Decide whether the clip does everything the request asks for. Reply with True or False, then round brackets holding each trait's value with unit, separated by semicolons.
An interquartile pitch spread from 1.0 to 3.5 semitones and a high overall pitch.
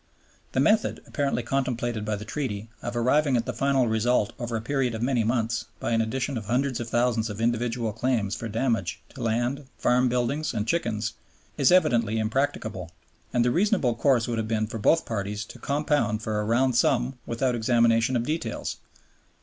False (2.8 semitones; 120 Hz)